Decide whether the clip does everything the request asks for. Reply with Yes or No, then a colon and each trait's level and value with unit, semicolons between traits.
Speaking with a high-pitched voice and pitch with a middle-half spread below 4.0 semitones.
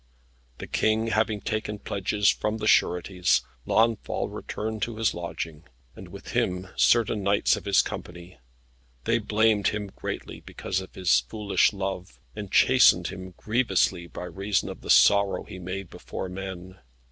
No: low, 100 Hz; average, 2.9 semitones